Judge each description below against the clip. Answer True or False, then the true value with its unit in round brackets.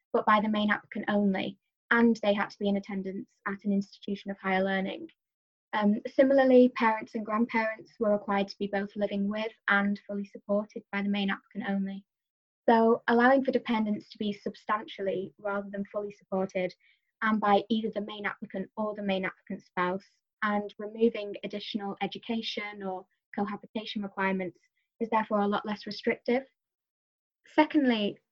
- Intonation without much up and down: True (2.1 semitones)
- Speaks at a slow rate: False (160 wpm)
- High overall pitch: True (205 Hz)